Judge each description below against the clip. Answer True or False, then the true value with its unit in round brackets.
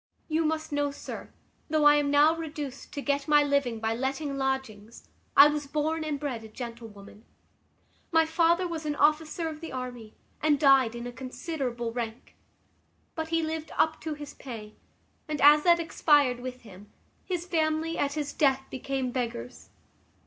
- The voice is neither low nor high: False (285 Hz)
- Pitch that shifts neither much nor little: True (4.1 semitones)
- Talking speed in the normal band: True (170 wpm)